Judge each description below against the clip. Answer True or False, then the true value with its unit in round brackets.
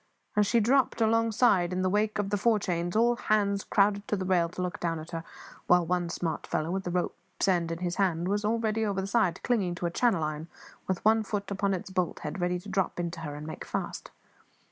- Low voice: False (190 Hz)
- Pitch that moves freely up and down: False (3.2 semitones)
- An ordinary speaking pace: False (235 wpm)